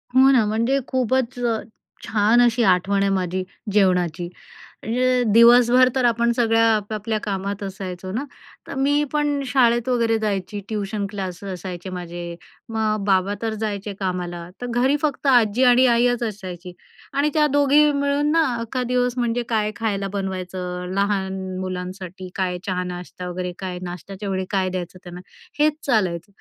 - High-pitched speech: Yes, high, 205 Hz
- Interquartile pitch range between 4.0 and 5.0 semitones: Yes, average, 4.7 semitones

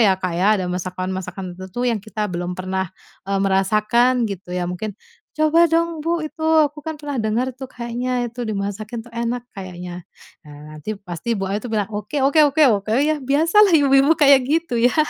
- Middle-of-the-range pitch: No, high, 225 Hz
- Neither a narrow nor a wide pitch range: No, wide, 6.6 semitones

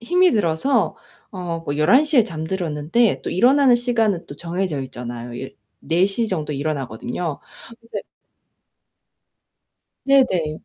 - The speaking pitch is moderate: Yes, medium, 175 Hz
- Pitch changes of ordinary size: No, wide, 7.6 semitones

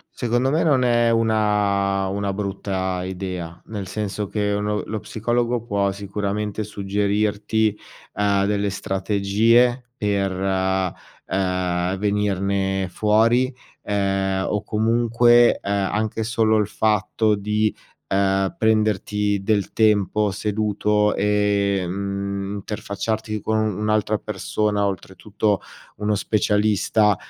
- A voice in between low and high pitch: No, low, 105 Hz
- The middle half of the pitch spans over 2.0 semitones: No, narrow, 1.7 semitones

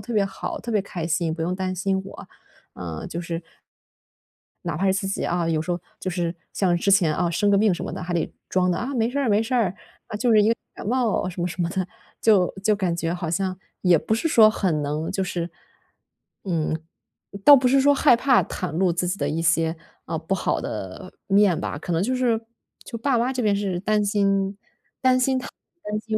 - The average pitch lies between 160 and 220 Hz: Yes, high, 190 Hz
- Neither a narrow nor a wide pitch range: Yes, average, 3.9 semitones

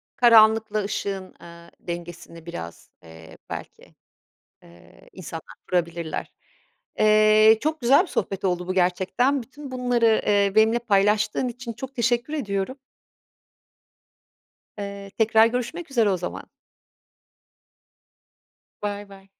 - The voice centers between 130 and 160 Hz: No, high, 210 Hz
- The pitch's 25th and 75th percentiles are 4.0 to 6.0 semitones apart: Yes, average, 4.3 semitones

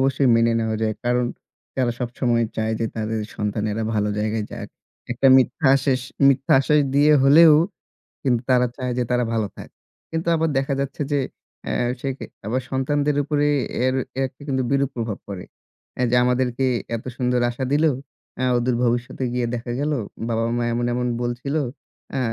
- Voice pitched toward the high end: No, low, 125 Hz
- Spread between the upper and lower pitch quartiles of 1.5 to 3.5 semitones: Yes, average, 2.8 semitones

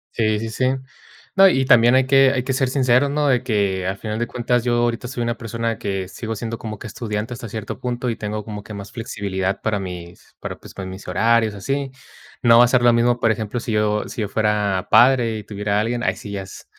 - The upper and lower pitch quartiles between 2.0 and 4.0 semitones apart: Yes, average, 2.9 semitones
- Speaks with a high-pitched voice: No, low, 115 Hz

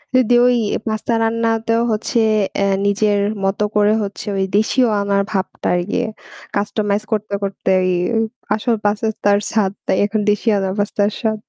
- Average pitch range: No, narrow, 1.8 semitones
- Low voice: No, high, 210 Hz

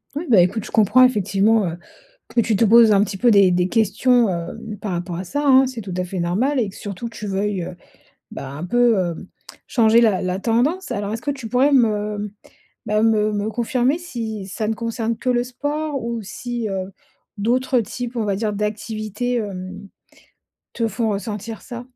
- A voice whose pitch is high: Yes, high, 220 Hz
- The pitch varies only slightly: No, average, 3.4 semitones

